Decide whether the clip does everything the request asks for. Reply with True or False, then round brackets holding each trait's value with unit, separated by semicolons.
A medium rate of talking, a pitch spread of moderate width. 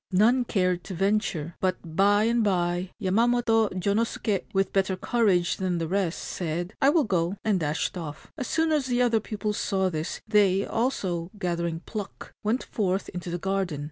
True (175 wpm; 3.9 semitones)